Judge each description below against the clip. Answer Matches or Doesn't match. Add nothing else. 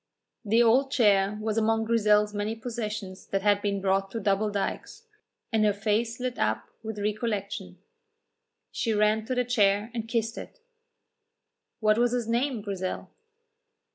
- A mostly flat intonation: Matches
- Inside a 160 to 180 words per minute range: Doesn't match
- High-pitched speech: Matches